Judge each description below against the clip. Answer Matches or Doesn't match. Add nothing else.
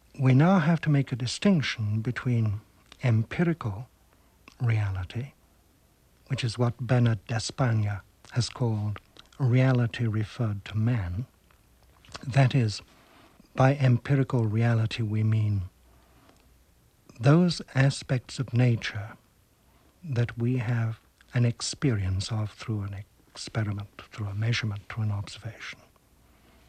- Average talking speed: Doesn't match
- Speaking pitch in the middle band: Doesn't match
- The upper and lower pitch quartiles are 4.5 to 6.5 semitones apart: Doesn't match